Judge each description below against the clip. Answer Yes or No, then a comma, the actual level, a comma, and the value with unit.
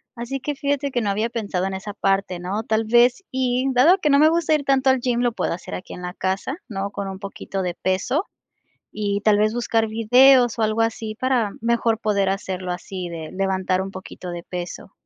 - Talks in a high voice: Yes, high, 215 Hz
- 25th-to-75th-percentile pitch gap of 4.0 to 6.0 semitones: Yes, average, 4.5 semitones